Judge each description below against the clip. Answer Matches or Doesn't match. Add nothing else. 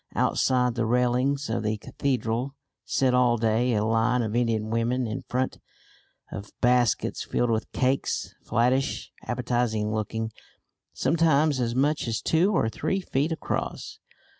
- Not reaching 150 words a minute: Matches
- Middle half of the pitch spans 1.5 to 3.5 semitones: Matches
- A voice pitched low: Matches